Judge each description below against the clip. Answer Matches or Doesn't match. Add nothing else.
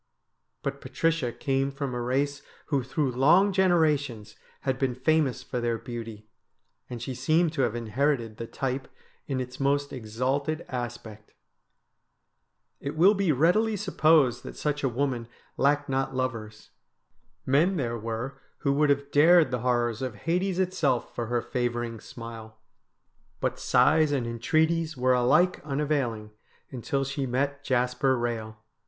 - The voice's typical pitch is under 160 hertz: Matches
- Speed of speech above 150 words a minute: Doesn't match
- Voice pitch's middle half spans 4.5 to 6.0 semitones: Doesn't match